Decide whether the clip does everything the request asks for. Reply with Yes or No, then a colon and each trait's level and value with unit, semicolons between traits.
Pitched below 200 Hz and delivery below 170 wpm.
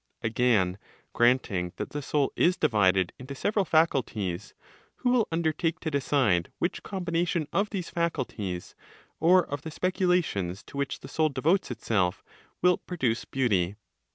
Yes: medium, 140 Hz; average, 140 wpm